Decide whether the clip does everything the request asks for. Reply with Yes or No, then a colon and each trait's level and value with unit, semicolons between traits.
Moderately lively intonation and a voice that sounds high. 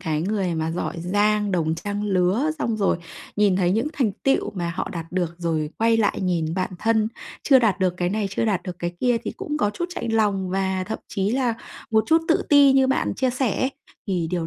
Yes: average, 4.2 semitones; high, 200 Hz